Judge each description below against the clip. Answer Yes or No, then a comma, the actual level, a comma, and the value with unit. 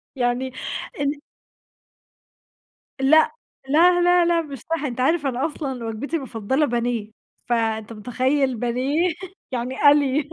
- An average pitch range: Yes, average, 4.0 semitones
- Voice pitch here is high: Yes, very high, 265 Hz